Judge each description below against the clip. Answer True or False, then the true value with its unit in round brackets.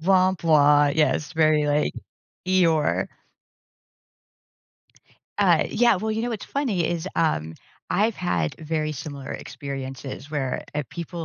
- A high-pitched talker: False (155 Hz)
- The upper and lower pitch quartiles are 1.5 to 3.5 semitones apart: False (4.0 semitones)